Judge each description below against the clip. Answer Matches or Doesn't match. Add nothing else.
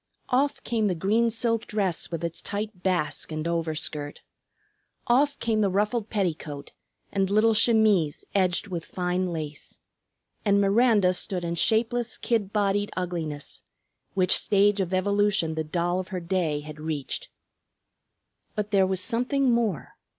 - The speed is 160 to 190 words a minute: Doesn't match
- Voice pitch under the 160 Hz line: Doesn't match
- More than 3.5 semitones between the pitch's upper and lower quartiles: Matches